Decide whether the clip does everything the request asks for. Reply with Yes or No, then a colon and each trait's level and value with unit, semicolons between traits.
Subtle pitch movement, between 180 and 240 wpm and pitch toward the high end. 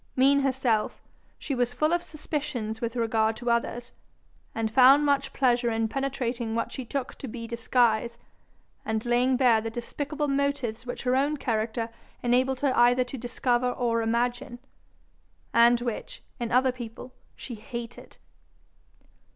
No: narrow, 2.3 semitones; average, 145 wpm; high, 245 Hz